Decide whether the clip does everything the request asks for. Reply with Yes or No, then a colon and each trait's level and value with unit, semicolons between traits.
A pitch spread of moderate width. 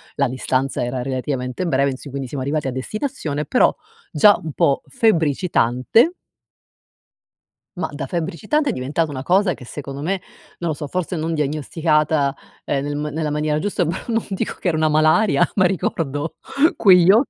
Yes: average, 4.4 semitones